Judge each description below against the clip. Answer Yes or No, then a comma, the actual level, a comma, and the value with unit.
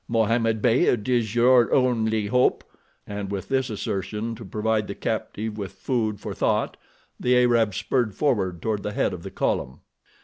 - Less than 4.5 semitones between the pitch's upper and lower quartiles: Yes, average, 2.8 semitones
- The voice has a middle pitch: No, low, 110 Hz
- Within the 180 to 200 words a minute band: No, average, 165 wpm